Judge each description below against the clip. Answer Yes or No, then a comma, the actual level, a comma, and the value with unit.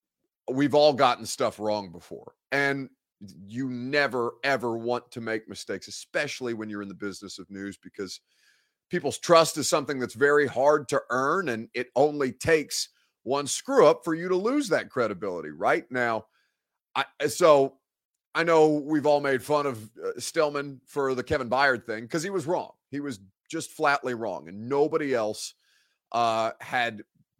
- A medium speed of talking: Yes, average, 165 wpm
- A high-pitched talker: No, low, 135 Hz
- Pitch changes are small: No, average, 4.4 semitones